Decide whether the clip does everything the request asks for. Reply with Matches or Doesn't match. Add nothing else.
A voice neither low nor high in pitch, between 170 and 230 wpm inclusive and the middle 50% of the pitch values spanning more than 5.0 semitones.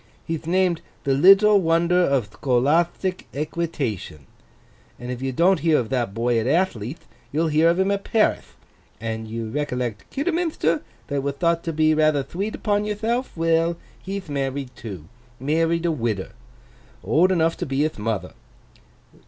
Doesn't match